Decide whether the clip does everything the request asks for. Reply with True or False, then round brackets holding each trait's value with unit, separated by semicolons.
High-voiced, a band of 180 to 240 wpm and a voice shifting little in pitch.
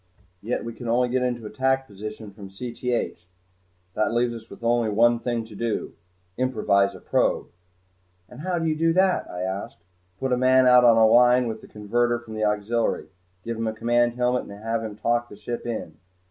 False (120 Hz; 200 wpm; 2.3 semitones)